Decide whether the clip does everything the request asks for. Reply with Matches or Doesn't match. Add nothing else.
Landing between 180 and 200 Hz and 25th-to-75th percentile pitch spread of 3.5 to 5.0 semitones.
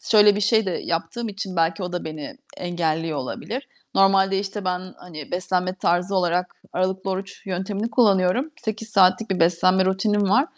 Doesn't match